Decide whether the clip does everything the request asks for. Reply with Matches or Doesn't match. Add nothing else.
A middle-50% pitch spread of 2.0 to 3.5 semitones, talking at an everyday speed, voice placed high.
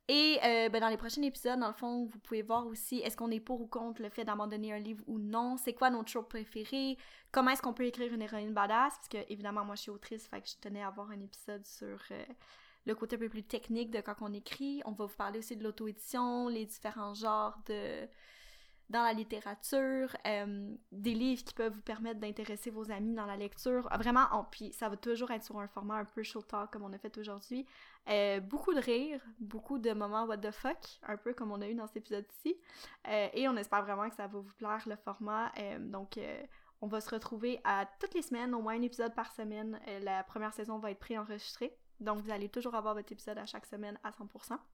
Doesn't match